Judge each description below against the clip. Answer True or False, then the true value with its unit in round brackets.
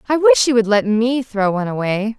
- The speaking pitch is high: True (220 Hz)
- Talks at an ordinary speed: False (245 wpm)